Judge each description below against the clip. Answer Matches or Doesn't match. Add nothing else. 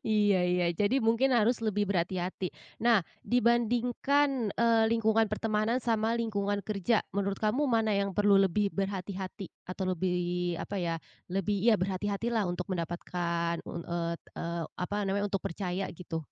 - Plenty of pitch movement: Doesn't match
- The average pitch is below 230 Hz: Matches